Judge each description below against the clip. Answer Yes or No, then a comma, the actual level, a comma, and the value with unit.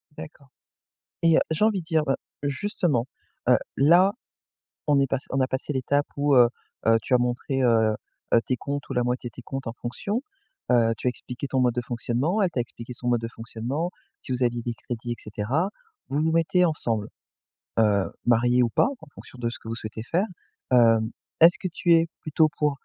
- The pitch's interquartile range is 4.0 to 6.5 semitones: Yes, average, 4.4 semitones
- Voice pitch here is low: Yes, low, 130 Hz